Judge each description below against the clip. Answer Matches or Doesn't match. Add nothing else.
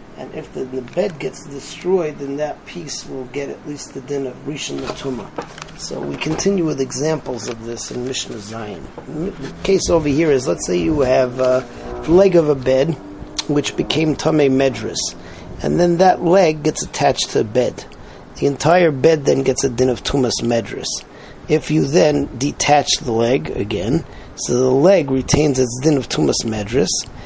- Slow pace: Doesn't match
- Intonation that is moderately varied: Matches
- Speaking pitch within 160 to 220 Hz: Doesn't match